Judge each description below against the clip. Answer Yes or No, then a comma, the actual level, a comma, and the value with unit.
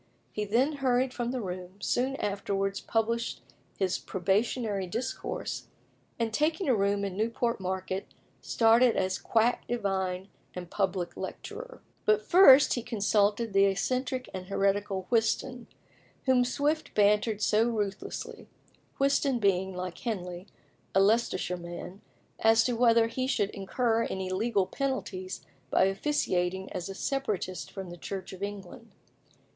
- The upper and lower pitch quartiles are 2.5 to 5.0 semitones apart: Yes, average, 4.1 semitones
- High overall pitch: Yes, high, 210 Hz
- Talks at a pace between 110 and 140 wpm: Yes, slow, 135 wpm